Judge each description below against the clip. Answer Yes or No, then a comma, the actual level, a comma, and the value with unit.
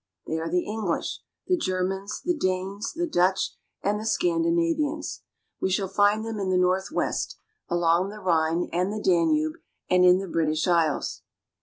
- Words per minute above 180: No, average, 160 wpm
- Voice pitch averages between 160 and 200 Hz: Yes, high, 190 Hz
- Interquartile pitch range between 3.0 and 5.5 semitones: Yes, average, 3.7 semitones